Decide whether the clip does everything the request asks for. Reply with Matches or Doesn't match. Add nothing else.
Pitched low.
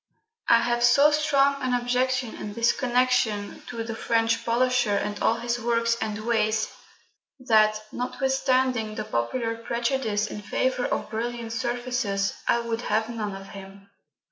Doesn't match